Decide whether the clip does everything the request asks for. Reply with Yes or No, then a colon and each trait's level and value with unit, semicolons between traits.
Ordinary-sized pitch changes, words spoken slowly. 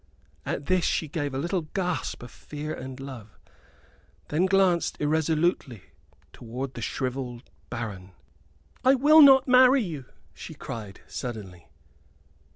No: wide, 7.0 semitones; slow, 125 wpm